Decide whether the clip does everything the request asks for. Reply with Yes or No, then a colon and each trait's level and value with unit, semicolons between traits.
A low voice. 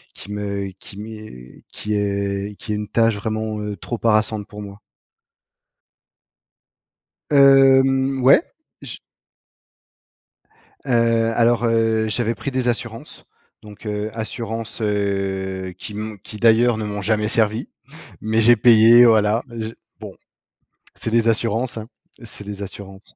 Yes: low, 110 Hz